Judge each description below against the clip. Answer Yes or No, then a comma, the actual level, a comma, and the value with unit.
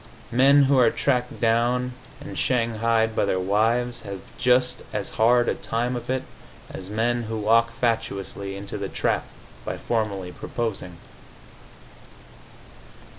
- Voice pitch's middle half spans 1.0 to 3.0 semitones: Yes, average, 2.7 semitones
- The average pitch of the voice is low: Yes, low, 115 Hz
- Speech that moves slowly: Yes, slow, 130 wpm